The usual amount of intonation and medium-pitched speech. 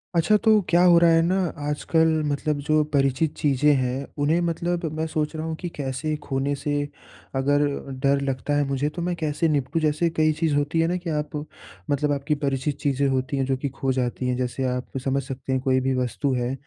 Yes: average, 3.0 semitones; medium, 145 Hz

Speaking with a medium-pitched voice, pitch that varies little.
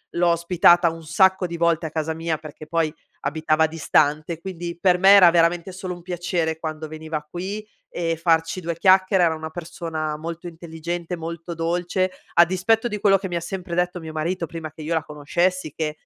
Yes: medium, 170 Hz; narrow, 1.9 semitones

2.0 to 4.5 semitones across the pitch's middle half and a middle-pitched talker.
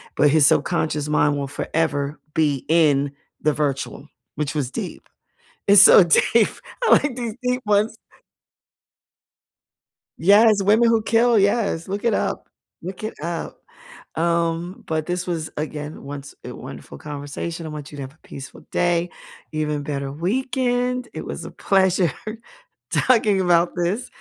No: wide, 5.6 semitones; medium, 170 Hz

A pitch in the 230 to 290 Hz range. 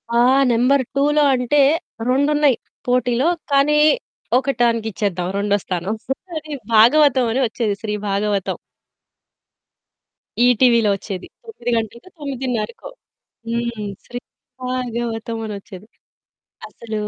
Yes: high, 235 Hz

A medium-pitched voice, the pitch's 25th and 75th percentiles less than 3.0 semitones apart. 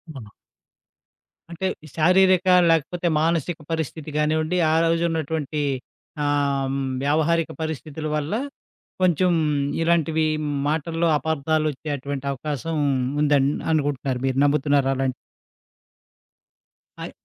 Yes: medium, 155 Hz; narrow, 2.5 semitones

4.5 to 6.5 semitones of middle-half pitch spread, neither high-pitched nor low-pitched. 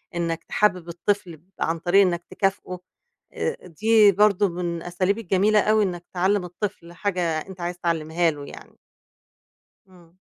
No: average, 2.9 semitones; medium, 180 Hz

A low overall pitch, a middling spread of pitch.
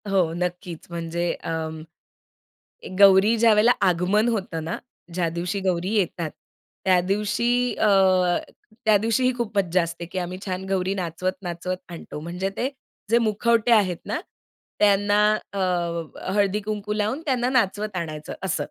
No: high, 190 Hz; average, 3.5 semitones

